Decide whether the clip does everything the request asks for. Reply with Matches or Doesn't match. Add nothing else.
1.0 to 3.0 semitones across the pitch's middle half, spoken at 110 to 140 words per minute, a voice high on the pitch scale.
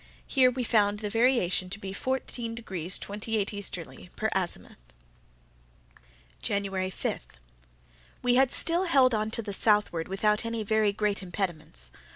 Doesn't match